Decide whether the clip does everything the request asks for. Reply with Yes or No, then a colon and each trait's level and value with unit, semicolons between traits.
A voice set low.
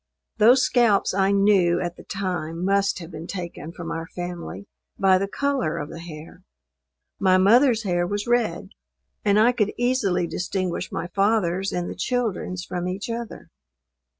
No: high, 190 Hz